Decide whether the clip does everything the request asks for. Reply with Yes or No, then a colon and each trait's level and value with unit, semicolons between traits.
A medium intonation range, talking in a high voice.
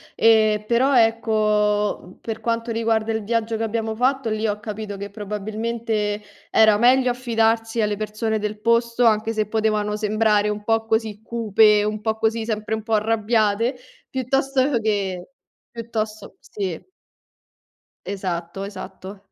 No: narrow, 1.6 semitones; high, 220 Hz